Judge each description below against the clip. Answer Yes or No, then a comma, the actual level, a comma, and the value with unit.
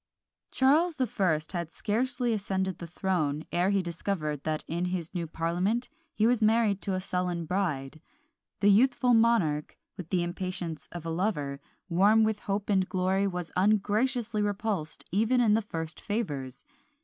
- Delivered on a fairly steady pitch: No, average, 4.3 semitones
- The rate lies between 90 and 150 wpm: No, average, 160 wpm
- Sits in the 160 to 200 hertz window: Yes, high, 190 Hz